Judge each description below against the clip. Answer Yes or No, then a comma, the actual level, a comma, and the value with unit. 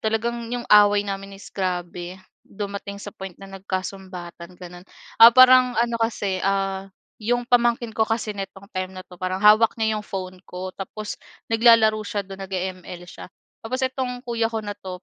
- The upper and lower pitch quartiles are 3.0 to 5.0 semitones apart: Yes, average, 3.3 semitones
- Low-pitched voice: No, high, 200 Hz